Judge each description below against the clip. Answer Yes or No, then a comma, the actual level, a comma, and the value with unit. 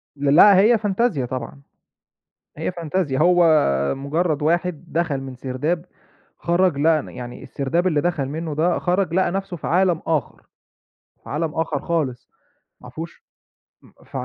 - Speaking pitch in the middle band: Yes, medium, 165 Hz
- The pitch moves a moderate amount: Yes, average, 3.9 semitones